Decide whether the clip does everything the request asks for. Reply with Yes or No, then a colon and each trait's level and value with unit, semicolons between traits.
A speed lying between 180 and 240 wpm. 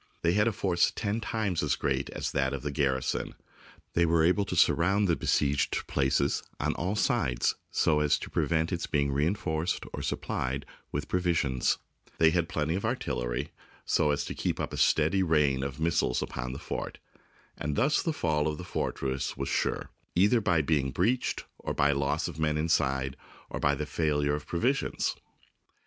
Yes: average, 190 wpm